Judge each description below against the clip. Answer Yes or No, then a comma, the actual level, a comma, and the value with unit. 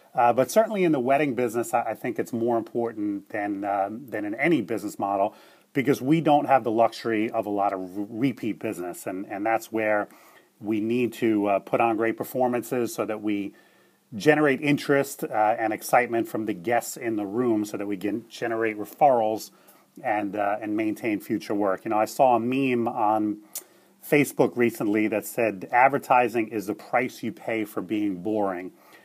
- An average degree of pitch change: Yes, average, 3.8 semitones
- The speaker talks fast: No, average, 190 wpm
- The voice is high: No, low, 115 Hz